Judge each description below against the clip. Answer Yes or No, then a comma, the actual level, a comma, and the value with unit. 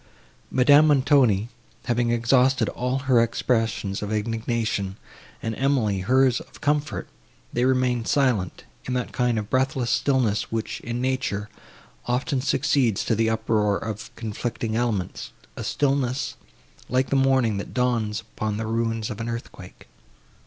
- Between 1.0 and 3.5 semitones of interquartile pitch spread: Yes, average, 3.0 semitones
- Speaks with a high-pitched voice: No, low, 120 Hz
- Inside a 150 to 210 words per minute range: No, average, 140 wpm